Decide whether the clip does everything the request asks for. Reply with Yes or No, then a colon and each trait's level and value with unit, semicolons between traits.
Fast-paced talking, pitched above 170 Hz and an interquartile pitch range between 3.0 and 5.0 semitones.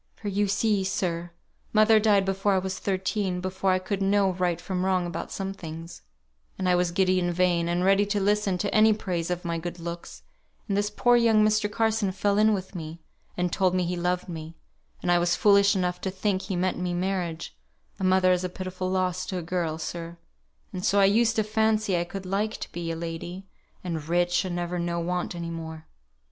No: fast, 215 wpm; medium, 185 Hz; narrow, 2.4 semitones